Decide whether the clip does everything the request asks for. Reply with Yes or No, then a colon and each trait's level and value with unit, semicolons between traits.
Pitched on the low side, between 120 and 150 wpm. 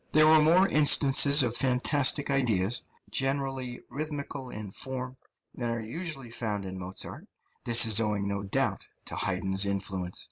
Yes: low, 125 Hz; average, 145 wpm